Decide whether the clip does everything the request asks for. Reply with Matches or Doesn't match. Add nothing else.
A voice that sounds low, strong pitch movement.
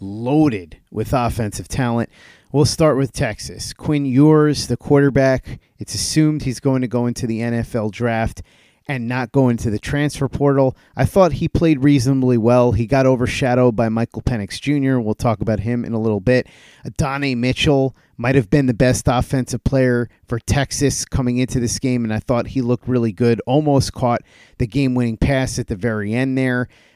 Doesn't match